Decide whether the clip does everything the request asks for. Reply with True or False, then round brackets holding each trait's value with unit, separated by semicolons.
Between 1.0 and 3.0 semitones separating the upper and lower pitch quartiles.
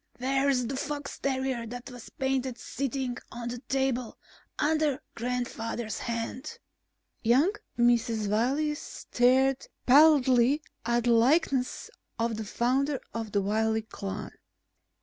True (2.6 semitones)